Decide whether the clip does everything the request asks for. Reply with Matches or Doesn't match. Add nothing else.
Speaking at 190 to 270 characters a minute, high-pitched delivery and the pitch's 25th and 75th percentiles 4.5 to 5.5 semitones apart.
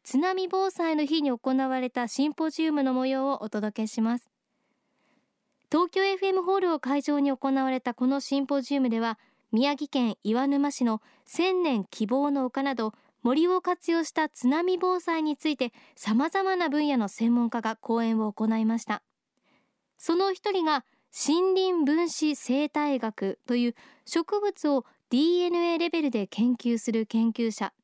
Doesn't match